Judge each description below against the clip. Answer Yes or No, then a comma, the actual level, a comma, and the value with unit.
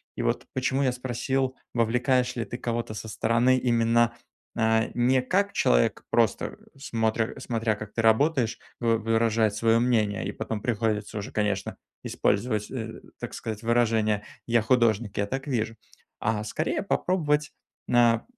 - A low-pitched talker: Yes, low, 115 Hz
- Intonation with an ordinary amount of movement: No, narrow, 2.2 semitones